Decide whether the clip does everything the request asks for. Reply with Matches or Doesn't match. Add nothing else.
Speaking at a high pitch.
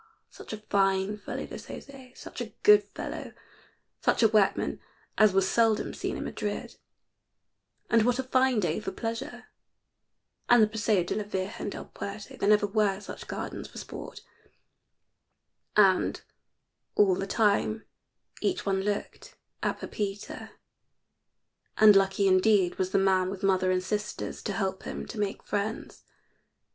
Matches